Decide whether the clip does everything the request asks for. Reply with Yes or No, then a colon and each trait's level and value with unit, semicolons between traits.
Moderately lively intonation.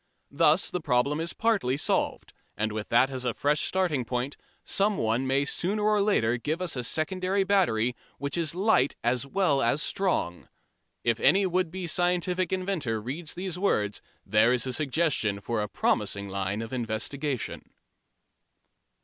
No: wide, 7.4 semitones